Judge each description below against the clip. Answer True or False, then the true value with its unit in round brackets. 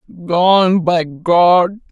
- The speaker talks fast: False (95 wpm)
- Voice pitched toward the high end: False (175 Hz)